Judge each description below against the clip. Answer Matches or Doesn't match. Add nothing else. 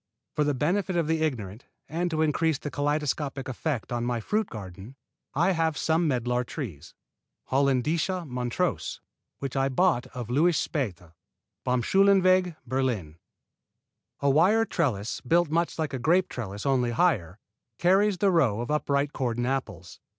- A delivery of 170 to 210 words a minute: Doesn't match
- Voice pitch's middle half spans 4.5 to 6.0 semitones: Matches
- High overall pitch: Doesn't match